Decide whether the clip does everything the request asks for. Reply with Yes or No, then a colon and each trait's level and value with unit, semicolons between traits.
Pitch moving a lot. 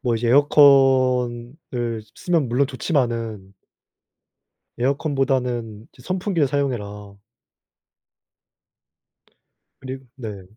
No: average, 3.2 semitones